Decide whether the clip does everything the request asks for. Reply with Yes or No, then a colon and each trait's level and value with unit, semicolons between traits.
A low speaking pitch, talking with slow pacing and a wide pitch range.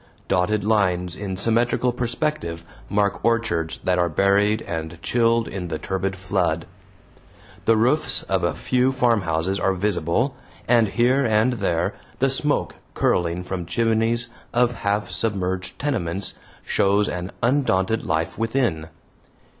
No: low, 100 Hz; slow, 130 wpm; average, 4.5 semitones